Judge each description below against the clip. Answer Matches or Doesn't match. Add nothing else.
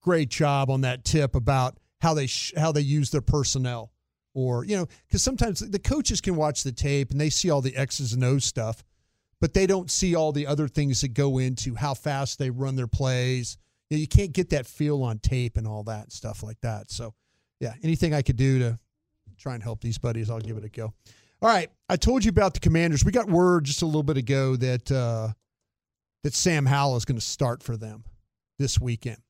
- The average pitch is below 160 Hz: Matches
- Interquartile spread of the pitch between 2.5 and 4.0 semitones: Doesn't match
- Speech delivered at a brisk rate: Matches